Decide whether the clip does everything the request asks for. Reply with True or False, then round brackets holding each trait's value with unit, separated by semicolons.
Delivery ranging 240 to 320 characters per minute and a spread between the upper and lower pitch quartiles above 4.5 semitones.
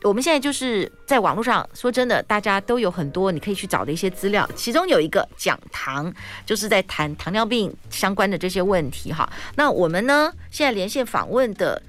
True (315 characters per minute; 4.9 semitones)